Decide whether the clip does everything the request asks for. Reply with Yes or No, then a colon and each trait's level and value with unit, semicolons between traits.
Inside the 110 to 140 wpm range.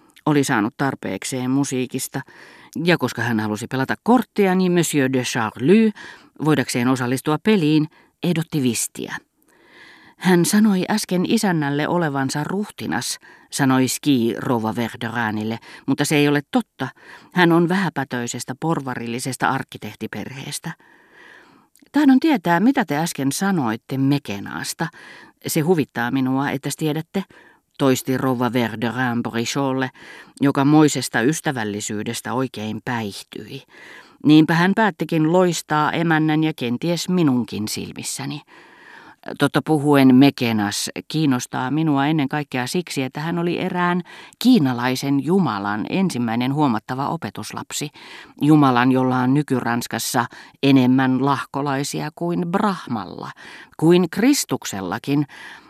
No: average, 100 wpm